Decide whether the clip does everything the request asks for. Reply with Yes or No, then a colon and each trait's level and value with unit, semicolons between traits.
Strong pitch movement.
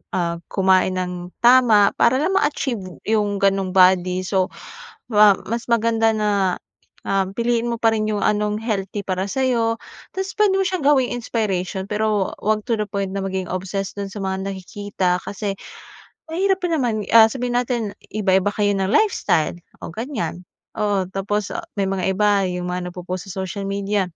No: average, 3.2 semitones